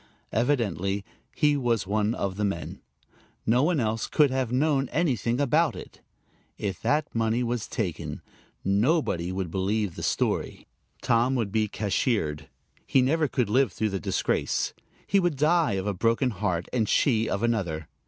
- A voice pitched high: No, low, 115 Hz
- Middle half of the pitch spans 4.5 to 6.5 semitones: Yes, average, 5.1 semitones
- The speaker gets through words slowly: No, average, 160 wpm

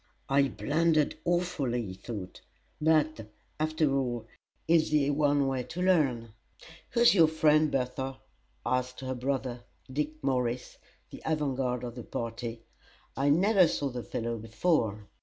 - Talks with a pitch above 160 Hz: No, low, 135 Hz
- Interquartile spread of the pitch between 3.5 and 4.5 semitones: Yes, average, 4.2 semitones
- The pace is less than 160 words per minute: Yes, average, 140 wpm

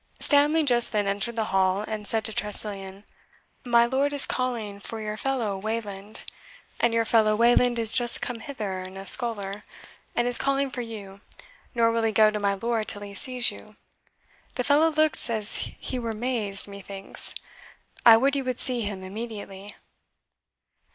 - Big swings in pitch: No, average, 3.2 semitones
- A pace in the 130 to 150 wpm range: No, average, 170 wpm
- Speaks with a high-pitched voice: Yes, high, 225 Hz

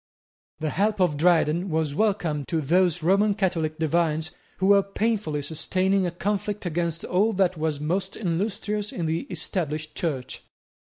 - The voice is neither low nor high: Yes, medium, 175 Hz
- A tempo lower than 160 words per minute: Yes, average, 150 wpm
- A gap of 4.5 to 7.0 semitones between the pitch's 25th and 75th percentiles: No, average, 3.9 semitones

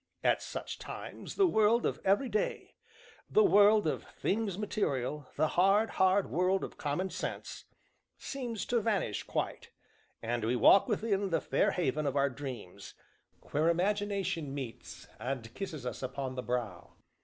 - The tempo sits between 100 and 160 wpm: Yes, average, 150 wpm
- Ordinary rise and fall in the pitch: No, wide, 7.6 semitones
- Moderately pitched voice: Yes, medium, 180 Hz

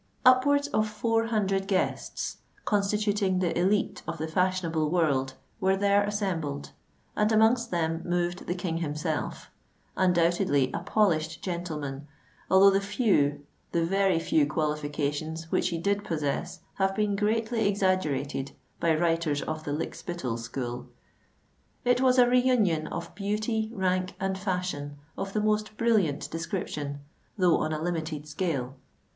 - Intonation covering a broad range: No, average, 4.7 semitones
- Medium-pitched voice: Yes, medium, 180 Hz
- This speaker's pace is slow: Yes, slow, 130 wpm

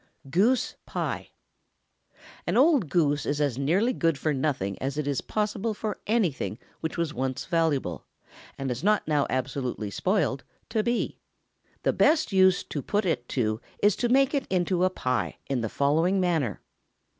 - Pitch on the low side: No, medium, 165 Hz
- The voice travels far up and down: Yes, wide, 7.3 semitones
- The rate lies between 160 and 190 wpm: Yes, average, 165 wpm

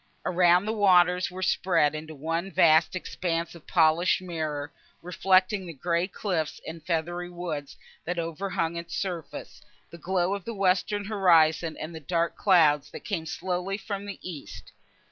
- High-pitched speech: No, medium, 175 Hz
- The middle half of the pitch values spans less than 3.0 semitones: Yes, narrow, 2.4 semitones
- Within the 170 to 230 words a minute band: No, average, 160 wpm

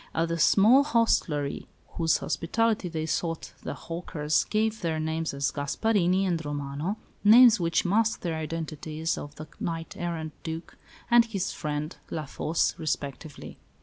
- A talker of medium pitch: Yes, medium, 165 Hz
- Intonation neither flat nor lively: Yes, average, 4.1 semitones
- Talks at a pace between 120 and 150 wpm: Yes, average, 145 wpm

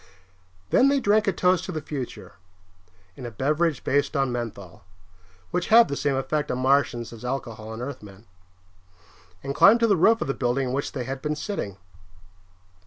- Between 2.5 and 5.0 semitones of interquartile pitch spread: No, wide, 5.5 semitones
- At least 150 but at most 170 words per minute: No, average, 180 wpm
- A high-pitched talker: No, low, 135 Hz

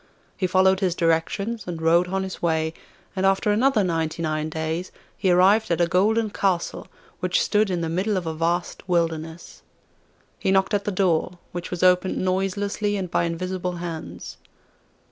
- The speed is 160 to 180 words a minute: Yes, average, 170 wpm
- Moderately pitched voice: Yes, medium, 180 Hz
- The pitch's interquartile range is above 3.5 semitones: No, narrow, 2.5 semitones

